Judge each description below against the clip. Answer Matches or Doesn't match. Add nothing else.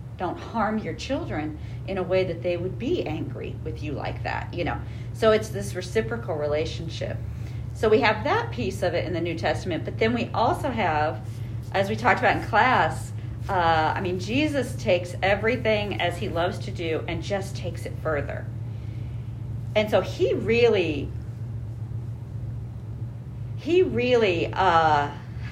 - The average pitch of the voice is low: Matches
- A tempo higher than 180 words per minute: Doesn't match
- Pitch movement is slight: Matches